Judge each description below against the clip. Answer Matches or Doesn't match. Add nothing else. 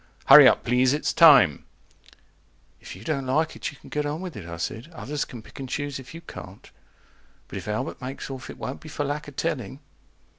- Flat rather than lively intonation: Doesn't match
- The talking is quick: Matches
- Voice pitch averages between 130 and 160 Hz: Matches